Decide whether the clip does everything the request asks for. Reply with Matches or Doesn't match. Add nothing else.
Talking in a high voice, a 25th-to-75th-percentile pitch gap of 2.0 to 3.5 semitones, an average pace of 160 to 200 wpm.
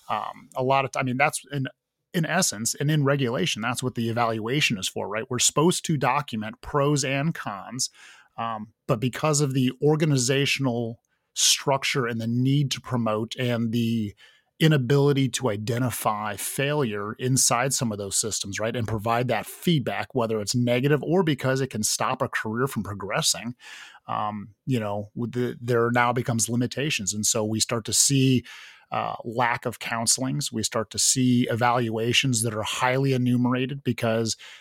Doesn't match